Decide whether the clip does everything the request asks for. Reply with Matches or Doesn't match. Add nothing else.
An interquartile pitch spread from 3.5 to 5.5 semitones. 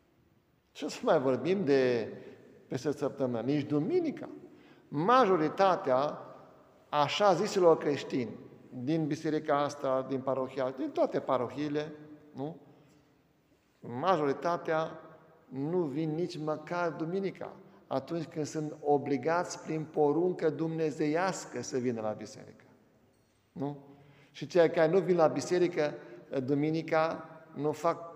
Doesn't match